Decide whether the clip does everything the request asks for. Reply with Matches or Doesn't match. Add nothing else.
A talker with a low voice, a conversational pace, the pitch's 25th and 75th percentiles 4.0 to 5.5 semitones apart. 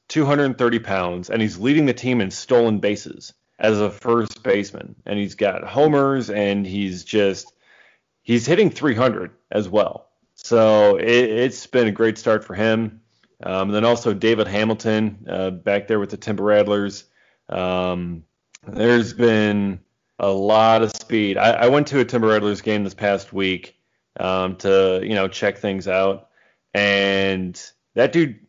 Doesn't match